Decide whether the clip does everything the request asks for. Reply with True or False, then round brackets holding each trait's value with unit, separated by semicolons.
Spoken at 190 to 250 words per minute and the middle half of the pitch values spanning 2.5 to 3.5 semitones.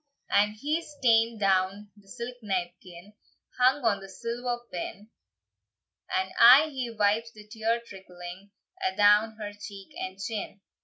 False (135 wpm; 3.2 semitones)